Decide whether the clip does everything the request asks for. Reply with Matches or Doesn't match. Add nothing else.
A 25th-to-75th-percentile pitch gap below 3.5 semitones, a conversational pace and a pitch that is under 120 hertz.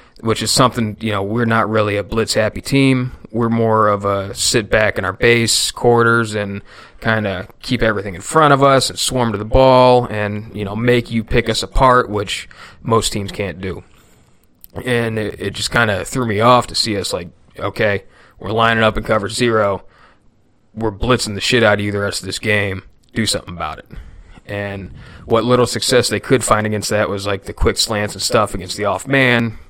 Doesn't match